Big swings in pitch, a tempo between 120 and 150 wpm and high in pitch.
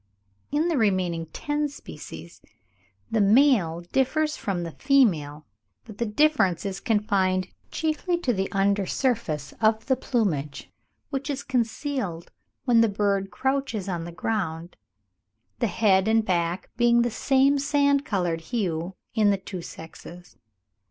Yes: wide, 6.8 semitones; average, 140 wpm; high, 210 Hz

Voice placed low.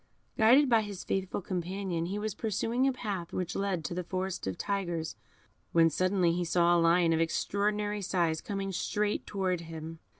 No: medium, 185 Hz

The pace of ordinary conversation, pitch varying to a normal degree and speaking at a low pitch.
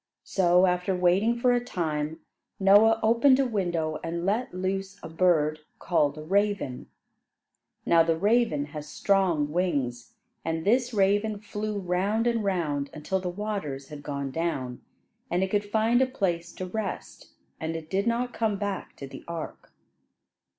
No: average, 155 wpm; average, 4.6 semitones; medium, 185 Hz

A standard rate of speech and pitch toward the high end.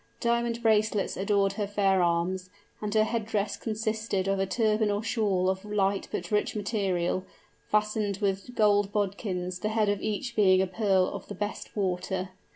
Yes: average, 170 wpm; high, 205 Hz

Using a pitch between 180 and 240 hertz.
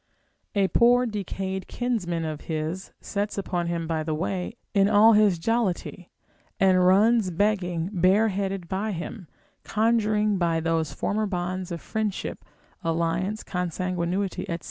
Yes: high, 190 Hz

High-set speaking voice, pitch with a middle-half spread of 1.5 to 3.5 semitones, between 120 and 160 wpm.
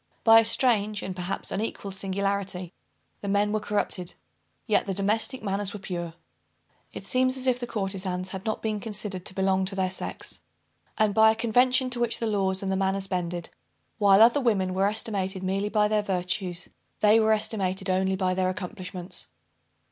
No: high, 200 Hz; narrow, 2.5 semitones; average, 180 wpm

